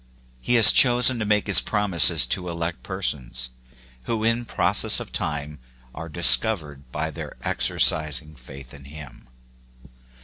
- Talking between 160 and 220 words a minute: No, slow, 135 wpm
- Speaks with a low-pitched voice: Yes, very low, 80 Hz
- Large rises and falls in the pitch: Yes, wide, 6.6 semitones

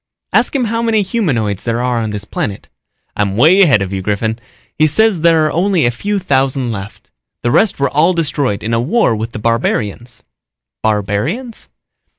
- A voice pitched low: Yes, low, 125 Hz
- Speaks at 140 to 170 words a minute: No, average, 180 wpm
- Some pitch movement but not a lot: No, wide, 8.5 semitones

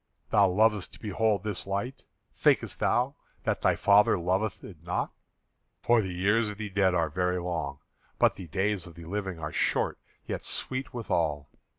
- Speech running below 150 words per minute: No, average, 175 wpm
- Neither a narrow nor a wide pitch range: Yes, average, 3.3 semitones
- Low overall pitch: Yes, very low, 95 Hz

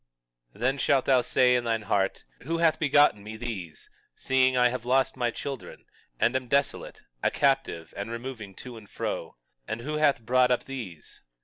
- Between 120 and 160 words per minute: No, average, 185 wpm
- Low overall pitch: Yes, low, 125 Hz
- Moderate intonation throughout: Yes, average, 3.1 semitones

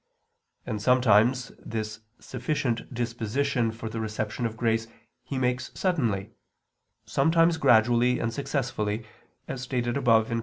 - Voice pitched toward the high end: No, low, 120 Hz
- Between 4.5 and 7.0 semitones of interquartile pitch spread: No, narrow, 2.5 semitones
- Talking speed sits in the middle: No, slow, 120 wpm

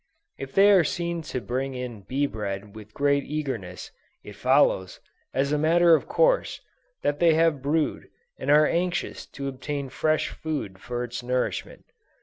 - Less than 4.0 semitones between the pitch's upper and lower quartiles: No, average, 4.4 semitones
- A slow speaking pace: No, average, 160 wpm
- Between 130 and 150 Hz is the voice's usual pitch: Yes, medium, 140 Hz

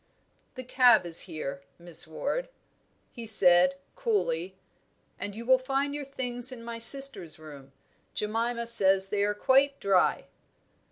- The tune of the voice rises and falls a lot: Yes, wide, 6.1 semitones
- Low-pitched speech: No, high, 230 Hz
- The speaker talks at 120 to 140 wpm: Yes, slow, 135 wpm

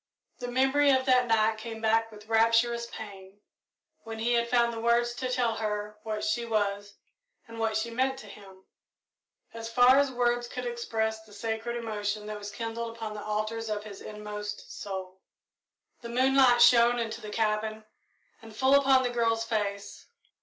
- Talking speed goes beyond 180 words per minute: No, average, 175 wpm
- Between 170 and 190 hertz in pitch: No, high, 225 Hz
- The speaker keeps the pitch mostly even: Yes, narrow, 2.0 semitones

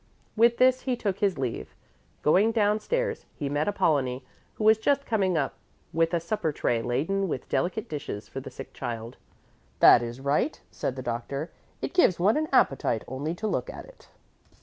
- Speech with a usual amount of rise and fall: No, wide, 8.3 semitones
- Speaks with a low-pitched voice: No, medium, 170 Hz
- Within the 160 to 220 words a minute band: Yes, average, 180 wpm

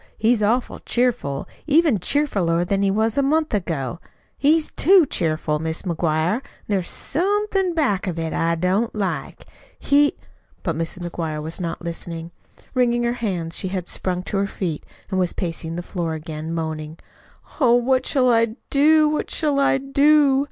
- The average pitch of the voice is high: Yes, high, 200 Hz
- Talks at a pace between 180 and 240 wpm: No, average, 165 wpm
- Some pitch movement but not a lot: No, wide, 8.4 semitones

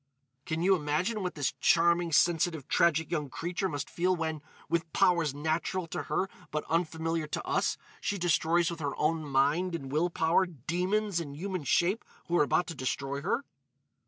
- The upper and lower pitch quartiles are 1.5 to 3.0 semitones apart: Yes, average, 2.7 semitones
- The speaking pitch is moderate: Yes, medium, 165 Hz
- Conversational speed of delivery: Yes, average, 175 wpm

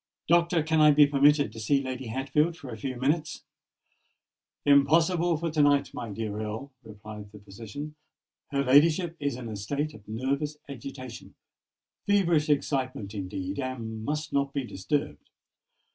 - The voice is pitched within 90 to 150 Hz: Yes, medium, 140 Hz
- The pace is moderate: Yes, average, 145 wpm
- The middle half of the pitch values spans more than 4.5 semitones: Yes, average, 5.1 semitones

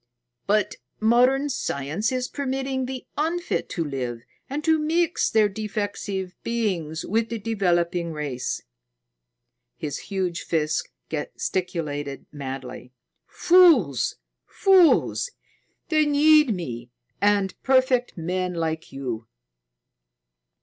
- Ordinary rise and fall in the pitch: No, wide, 8.8 semitones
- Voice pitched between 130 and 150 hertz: No, high, 200 Hz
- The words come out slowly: Yes, slow, 100 wpm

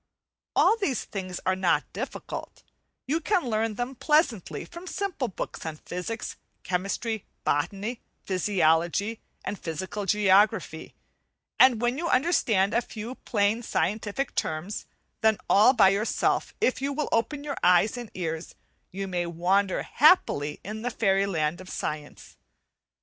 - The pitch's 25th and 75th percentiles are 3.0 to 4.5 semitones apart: No, average, 4.9 semitones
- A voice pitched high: Yes, high, 210 Hz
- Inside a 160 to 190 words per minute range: No, average, 140 wpm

